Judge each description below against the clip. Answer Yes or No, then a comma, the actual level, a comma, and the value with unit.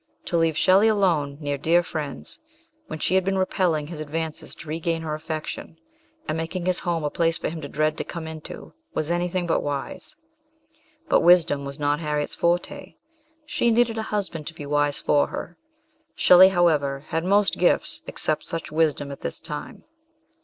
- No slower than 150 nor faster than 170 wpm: No, average, 180 wpm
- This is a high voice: No, medium, 165 Hz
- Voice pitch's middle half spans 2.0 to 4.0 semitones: Yes, average, 2.8 semitones